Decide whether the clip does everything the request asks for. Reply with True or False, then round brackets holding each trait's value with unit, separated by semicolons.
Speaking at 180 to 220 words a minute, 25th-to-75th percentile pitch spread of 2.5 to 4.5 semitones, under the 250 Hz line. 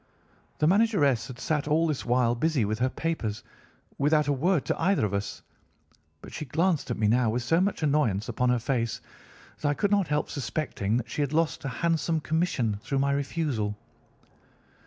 False (190 wpm; 5.2 semitones; 140 Hz)